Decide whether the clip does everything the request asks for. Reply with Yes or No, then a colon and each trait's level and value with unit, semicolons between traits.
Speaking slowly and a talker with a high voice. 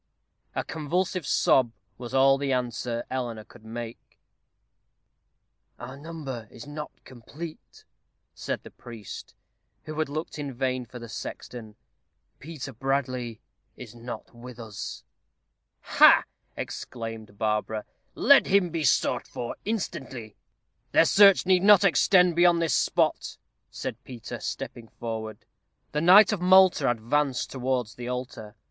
No: slow, 125 wpm; low, 130 Hz